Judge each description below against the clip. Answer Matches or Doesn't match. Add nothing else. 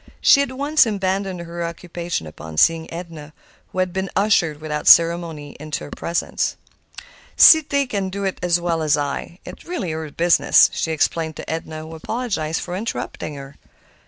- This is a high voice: Doesn't match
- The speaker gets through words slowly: Doesn't match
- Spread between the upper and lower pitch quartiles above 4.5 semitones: Doesn't match